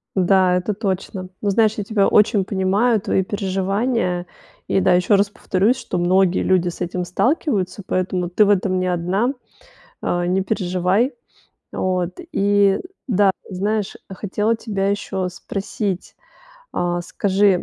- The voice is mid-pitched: No, high, 195 Hz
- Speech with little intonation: Yes, narrow, 2.2 semitones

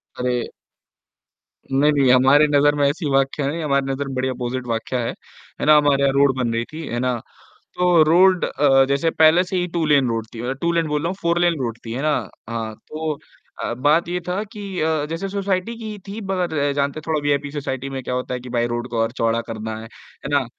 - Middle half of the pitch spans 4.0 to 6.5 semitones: Yes, average, 4.5 semitones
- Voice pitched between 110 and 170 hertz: Yes, medium, 140 Hz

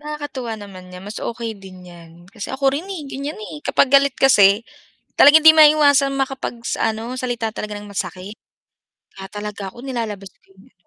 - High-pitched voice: Yes, high, 230 Hz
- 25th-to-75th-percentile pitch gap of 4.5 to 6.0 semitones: Yes, wide, 5.5 semitones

